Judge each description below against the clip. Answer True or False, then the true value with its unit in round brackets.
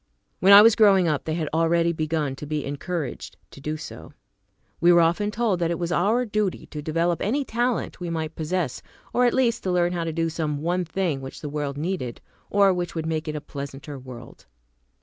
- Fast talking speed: True (215 wpm)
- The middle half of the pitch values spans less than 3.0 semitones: False (3.7 semitones)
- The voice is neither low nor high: True (170 Hz)